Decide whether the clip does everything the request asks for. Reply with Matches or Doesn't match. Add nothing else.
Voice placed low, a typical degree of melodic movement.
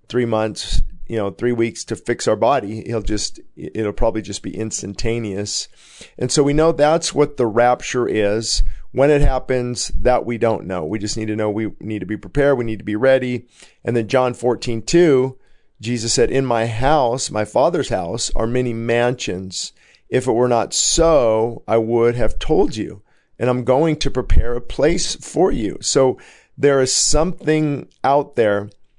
Matches